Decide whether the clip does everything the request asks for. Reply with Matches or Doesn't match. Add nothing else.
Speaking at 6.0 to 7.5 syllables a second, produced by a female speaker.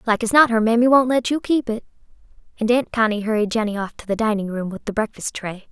Matches